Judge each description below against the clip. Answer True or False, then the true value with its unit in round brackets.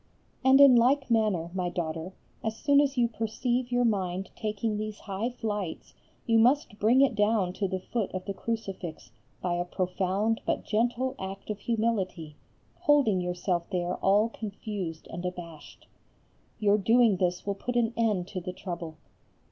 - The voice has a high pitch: True (205 Hz)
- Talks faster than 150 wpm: True (165 wpm)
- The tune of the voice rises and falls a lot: False (4.2 semitones)